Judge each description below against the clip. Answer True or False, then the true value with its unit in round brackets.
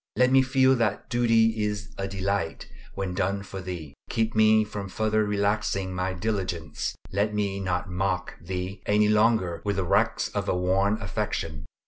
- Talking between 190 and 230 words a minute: False (165 wpm)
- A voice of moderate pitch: False (100 Hz)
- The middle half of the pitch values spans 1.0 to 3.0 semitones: True (2.7 semitones)